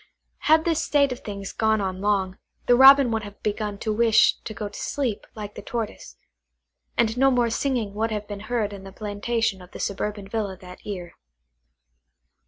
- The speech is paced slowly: No, average, 190 wpm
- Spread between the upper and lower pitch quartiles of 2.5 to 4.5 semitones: Yes, average, 2.9 semitones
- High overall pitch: Yes, high, 215 Hz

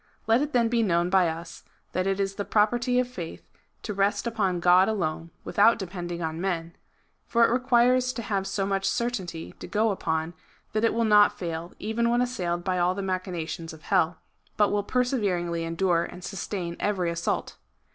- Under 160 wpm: No, average, 185 wpm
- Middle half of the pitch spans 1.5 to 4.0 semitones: No, average, 4.6 semitones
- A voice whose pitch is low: No, high, 195 Hz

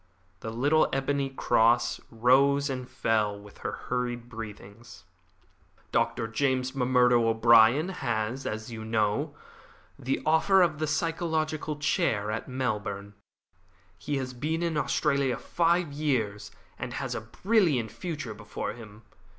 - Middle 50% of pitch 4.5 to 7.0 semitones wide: Yes, average, 5.0 semitones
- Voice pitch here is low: Yes, low, 125 Hz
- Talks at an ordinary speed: No, slow, 125 wpm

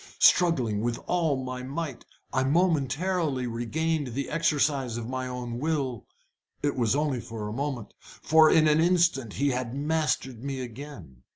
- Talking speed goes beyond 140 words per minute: Yes, average, 155 wpm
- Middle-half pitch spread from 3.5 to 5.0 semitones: Yes, average, 4.2 semitones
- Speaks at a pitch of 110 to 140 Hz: Yes, low, 135 Hz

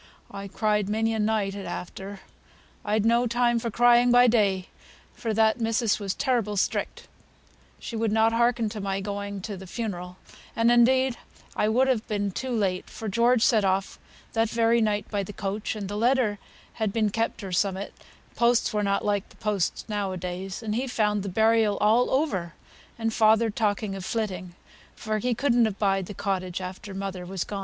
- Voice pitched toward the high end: Yes, high, 215 Hz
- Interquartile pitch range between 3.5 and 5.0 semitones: No, average, 2.8 semitones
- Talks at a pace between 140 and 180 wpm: No, average, 190 wpm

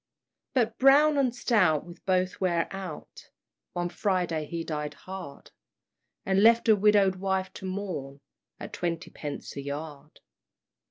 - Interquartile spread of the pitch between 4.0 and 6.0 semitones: Yes, average, 4.3 semitones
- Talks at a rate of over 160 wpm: No, average, 140 wpm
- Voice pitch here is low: No, medium, 185 Hz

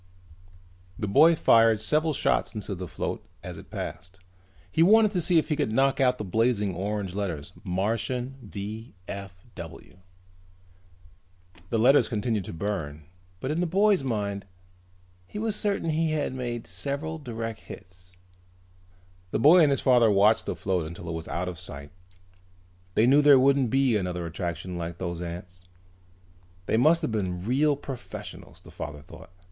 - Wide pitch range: Yes, wide, 7.3 semitones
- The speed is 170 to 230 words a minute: No, average, 160 wpm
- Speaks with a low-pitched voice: Yes, low, 110 Hz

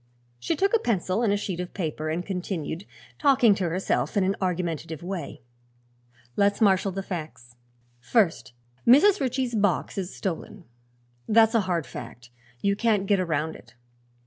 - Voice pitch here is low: No, high, 190 Hz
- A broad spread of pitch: No, average, 4.3 semitones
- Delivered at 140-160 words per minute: Yes, average, 150 wpm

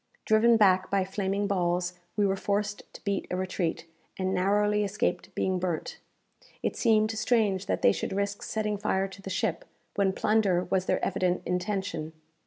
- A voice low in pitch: No, high, 195 Hz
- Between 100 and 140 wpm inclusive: No, average, 170 wpm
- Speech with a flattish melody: Yes, narrow, 2.0 semitones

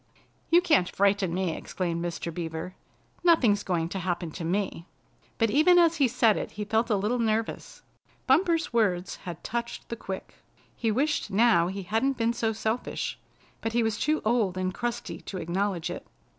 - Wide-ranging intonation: No, average, 4.7 semitones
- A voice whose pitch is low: No, high, 210 Hz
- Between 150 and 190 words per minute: Yes, average, 175 wpm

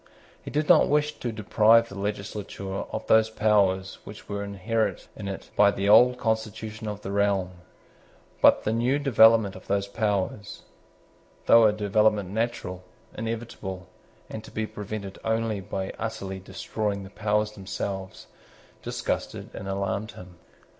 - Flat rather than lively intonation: Yes, narrow, 2.2 semitones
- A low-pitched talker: Yes, low, 105 Hz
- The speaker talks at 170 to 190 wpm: No, average, 145 wpm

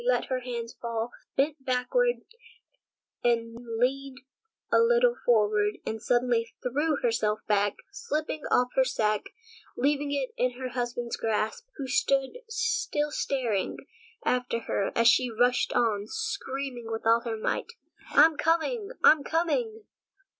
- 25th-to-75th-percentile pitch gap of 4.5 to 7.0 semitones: Yes, average, 5.0 semitones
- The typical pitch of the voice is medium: No, very high, 255 Hz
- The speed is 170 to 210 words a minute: No, average, 140 wpm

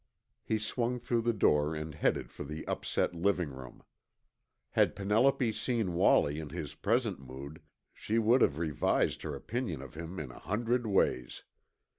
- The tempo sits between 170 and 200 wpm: No, average, 160 wpm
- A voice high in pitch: No, very low, 90 Hz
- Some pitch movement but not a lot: No, wide, 7.4 semitones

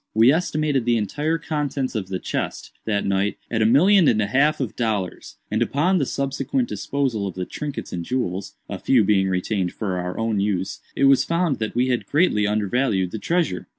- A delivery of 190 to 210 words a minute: Yes, average, 200 wpm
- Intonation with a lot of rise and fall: Yes, wide, 6.0 semitones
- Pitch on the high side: No, low, 115 Hz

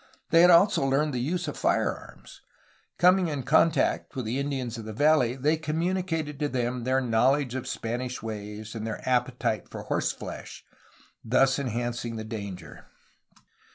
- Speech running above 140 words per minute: Yes, average, 155 wpm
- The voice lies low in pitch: Yes, low, 130 Hz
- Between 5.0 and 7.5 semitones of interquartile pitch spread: No, average, 4.5 semitones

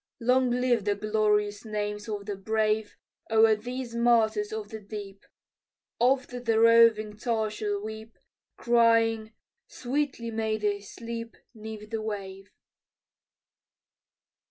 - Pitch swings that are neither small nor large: No, narrow, 1.8 semitones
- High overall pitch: Yes, high, 220 Hz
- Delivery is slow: Yes, slow, 115 wpm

